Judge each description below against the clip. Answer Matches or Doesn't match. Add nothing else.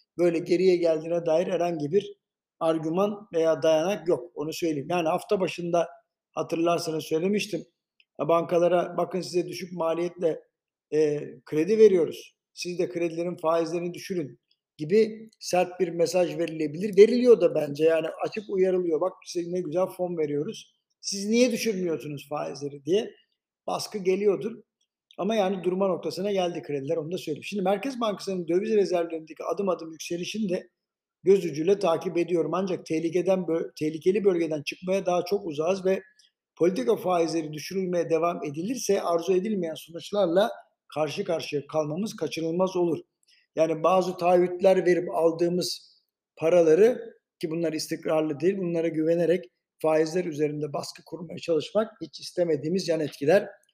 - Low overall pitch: Doesn't match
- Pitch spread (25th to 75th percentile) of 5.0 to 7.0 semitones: Doesn't match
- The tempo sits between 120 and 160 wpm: Matches